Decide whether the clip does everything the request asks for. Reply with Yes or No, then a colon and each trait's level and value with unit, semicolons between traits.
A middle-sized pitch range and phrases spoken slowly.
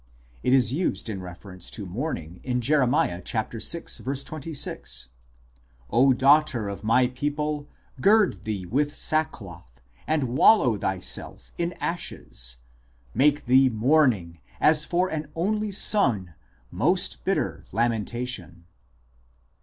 No: wide, 7.2 semitones; slow, 115 wpm